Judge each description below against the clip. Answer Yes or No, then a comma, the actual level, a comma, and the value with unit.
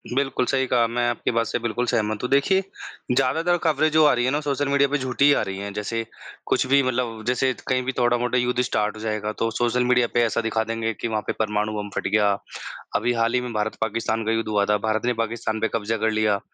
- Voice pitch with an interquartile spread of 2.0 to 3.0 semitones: Yes, average, 2.7 semitones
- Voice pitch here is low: Yes, low, 115 Hz